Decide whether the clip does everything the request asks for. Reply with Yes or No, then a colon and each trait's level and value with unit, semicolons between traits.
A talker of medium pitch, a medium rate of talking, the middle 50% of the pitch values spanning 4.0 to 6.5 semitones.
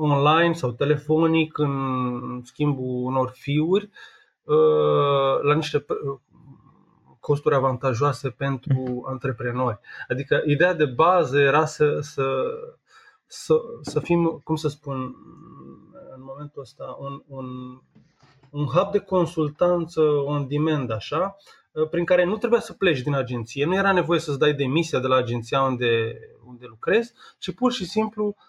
Yes: medium, 145 Hz; average, 130 wpm; average, 4.3 semitones